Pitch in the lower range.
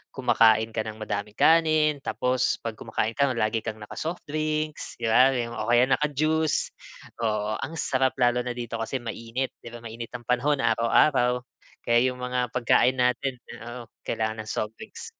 Yes: low, 125 Hz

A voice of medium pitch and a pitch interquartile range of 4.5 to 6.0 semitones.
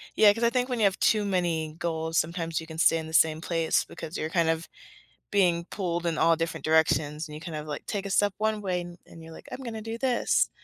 No: medium, 170 Hz; average, 4.1 semitones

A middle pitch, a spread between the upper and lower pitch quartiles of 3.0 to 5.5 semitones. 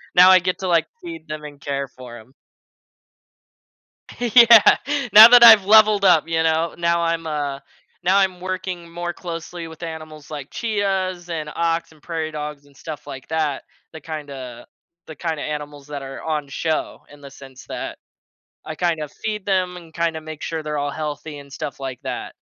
Yes: medium, 160 Hz; average, 3.3 semitones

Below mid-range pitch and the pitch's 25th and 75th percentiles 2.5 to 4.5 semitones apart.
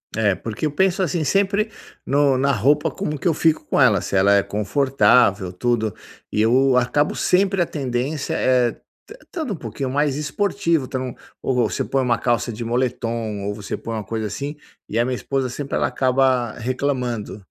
Yes: low, 130 Hz; average, 4.2 semitones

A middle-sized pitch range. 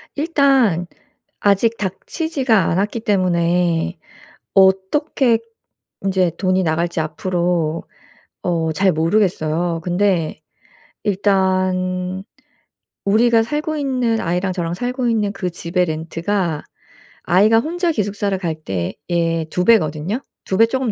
Yes: average, 4.7 semitones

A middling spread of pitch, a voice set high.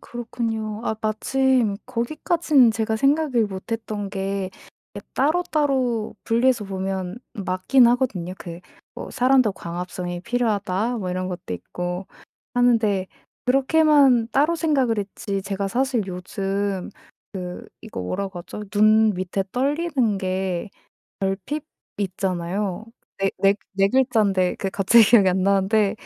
Yes: average, 4.4 semitones; high, 210 Hz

